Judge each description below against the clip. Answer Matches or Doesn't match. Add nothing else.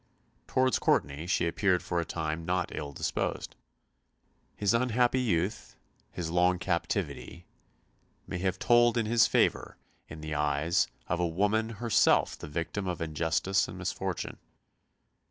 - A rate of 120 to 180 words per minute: Matches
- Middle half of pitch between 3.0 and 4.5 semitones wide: Doesn't match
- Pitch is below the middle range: Matches